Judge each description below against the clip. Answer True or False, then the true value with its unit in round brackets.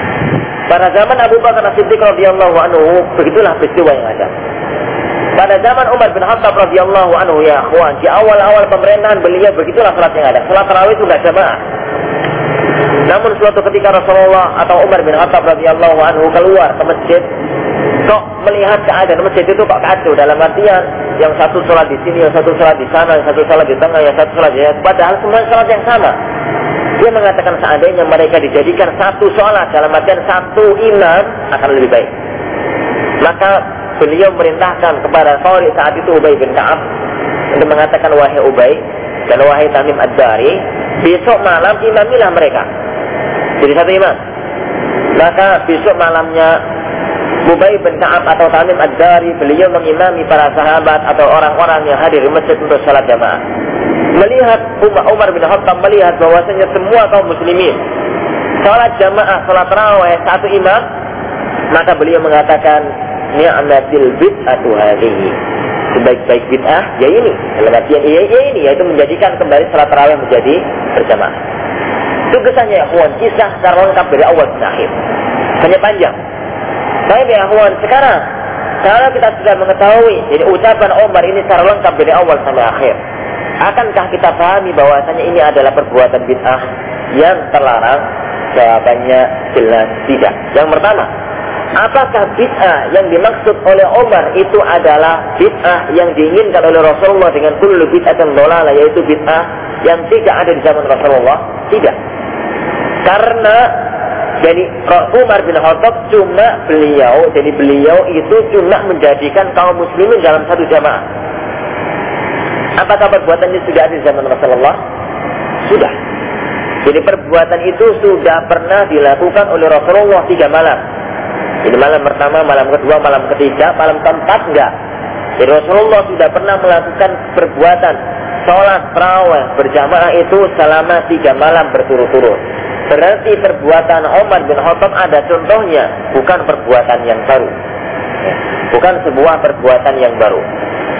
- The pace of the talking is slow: False (135 wpm)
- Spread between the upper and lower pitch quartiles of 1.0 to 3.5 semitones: False (4.9 semitones)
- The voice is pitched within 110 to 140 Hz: False (175 Hz)